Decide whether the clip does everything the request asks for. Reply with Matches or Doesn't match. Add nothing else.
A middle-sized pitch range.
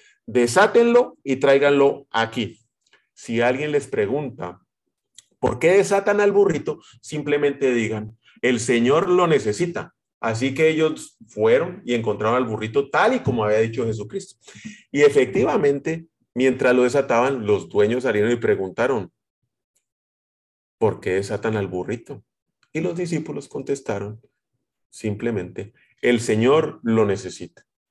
Doesn't match